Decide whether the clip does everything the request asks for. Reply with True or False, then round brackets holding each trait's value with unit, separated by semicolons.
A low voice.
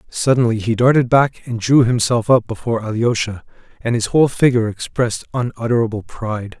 True (115 Hz)